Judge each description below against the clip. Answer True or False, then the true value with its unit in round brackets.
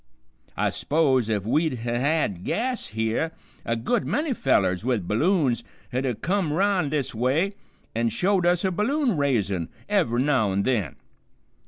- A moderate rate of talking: True (155 wpm)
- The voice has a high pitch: False (135 Hz)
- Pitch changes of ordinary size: False (8.0 semitones)